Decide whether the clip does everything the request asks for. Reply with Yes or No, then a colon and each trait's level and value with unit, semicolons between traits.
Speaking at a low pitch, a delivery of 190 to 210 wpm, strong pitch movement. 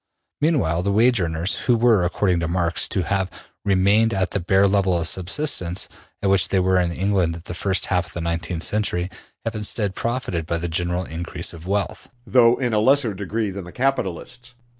No: very low, 95 Hz; fast, 205 wpm; average, 3.7 semitones